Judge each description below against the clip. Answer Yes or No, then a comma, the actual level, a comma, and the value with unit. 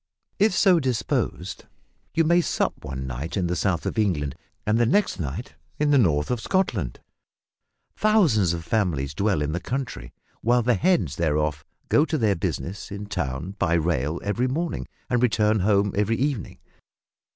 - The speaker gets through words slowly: No, average, 165 wpm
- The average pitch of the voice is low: Yes, low, 100 Hz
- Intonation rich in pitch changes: Yes, wide, 7.6 semitones